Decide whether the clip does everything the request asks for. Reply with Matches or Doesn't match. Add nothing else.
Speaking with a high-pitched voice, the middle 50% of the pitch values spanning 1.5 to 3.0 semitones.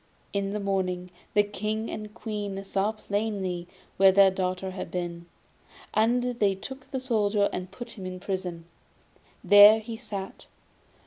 Matches